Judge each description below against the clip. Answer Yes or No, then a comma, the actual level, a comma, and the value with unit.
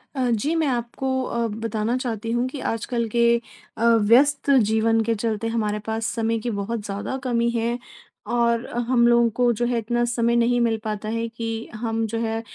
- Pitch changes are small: Yes, narrow, 1.2 semitones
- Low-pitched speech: No, high, 230 Hz